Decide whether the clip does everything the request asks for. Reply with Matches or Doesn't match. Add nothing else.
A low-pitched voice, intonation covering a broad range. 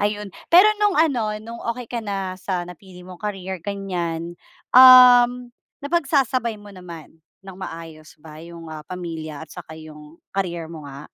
Doesn't match